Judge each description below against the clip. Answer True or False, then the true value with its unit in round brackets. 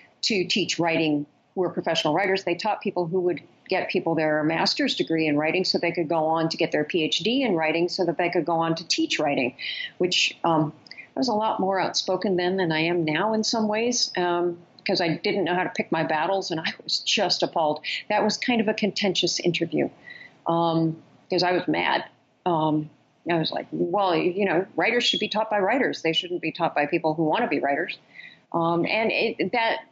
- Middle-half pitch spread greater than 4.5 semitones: False (3.3 semitones)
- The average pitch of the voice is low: False (175 Hz)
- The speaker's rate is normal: False (220 wpm)